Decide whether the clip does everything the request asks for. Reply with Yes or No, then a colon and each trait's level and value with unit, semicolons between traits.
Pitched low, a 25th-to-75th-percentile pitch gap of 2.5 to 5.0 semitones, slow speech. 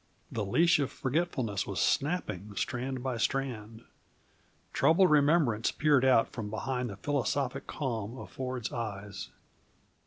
Yes: low, 130 Hz; average, 4.4 semitones; slow, 125 wpm